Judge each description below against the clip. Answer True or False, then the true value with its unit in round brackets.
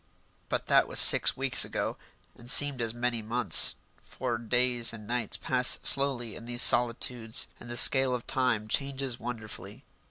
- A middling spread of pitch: False (1.6 semitones)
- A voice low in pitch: True (120 Hz)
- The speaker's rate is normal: True (160 wpm)